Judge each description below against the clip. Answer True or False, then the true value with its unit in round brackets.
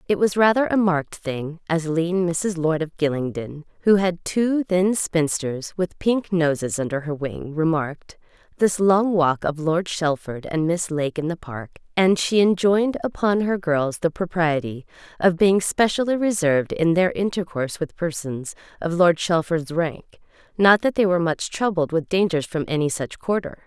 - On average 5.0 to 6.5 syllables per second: False (4.6 syllables/s)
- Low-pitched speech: False (170 Hz)